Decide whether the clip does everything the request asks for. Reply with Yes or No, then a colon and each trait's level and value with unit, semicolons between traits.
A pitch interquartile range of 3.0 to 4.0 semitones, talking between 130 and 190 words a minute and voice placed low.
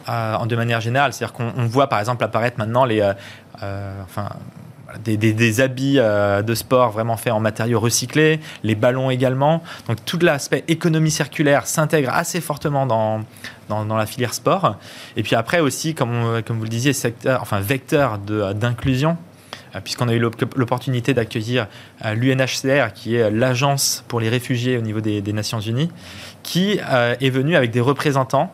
Yes: average, 3.6 semitones; average, 175 wpm; low, 125 Hz